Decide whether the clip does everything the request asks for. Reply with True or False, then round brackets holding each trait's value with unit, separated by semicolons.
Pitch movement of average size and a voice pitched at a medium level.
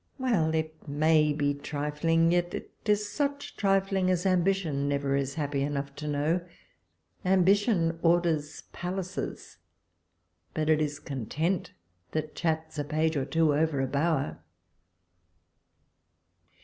True (3.5 semitones; 160 Hz)